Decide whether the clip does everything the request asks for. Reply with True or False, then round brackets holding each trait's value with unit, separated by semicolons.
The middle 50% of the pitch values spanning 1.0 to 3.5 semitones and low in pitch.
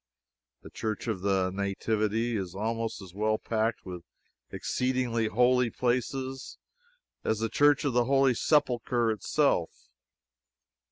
True (3.1 semitones; 115 Hz)